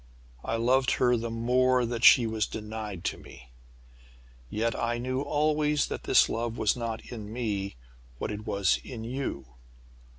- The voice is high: No, low, 115 Hz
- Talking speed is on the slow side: No, average, 160 wpm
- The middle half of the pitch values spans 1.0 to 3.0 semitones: Yes, average, 2.7 semitones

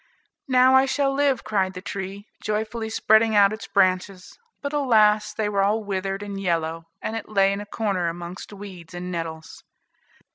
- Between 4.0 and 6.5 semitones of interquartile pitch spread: No, average, 2.9 semitones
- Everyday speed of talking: Yes, average, 175 wpm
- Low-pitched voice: No, high, 200 Hz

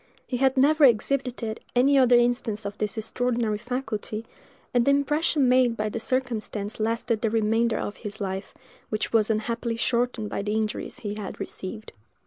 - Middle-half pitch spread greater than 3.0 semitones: No, average, 2.7 semitones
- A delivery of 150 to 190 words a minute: Yes, average, 165 wpm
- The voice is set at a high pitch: Yes, high, 230 Hz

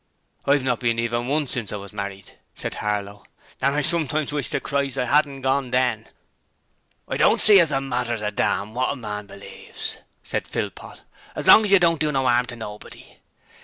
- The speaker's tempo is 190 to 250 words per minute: Yes, average, 200 wpm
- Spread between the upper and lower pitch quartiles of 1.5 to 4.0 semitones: No, average, 4.5 semitones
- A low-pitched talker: Yes, low, 125 Hz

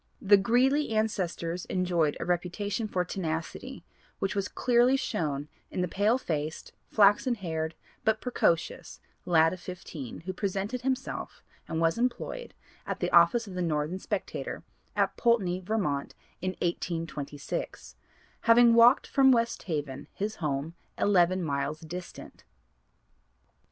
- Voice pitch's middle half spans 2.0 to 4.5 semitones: No, average, 5.2 semitones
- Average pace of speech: No, slow, 130 wpm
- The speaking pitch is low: No, medium, 185 Hz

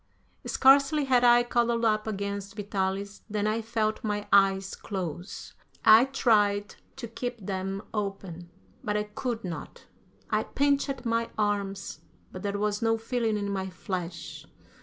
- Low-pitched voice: No, high, 210 Hz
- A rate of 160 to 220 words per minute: No, average, 140 wpm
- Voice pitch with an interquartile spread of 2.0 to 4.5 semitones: Yes, average, 2.8 semitones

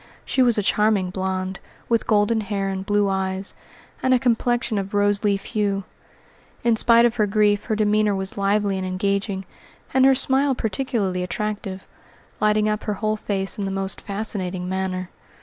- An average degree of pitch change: No, narrow, 2.1 semitones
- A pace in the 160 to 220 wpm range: Yes, average, 170 wpm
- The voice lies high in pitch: Yes, high, 205 Hz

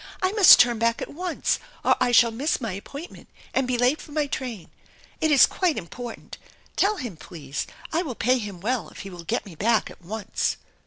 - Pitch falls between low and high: No, high, 240 Hz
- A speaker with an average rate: No, fast, 210 wpm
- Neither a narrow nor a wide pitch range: No, wide, 5.9 semitones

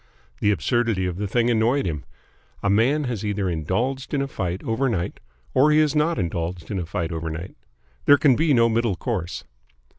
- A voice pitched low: Yes, low, 110 Hz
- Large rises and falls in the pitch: Yes, wide, 6.4 semitones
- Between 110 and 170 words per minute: No, average, 185 wpm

